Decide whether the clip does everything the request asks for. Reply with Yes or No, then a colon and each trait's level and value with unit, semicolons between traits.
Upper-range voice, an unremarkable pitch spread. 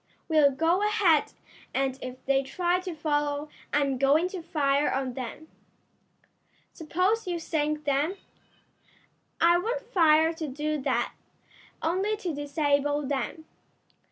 Yes: very high, 305 Hz; average, 3.6 semitones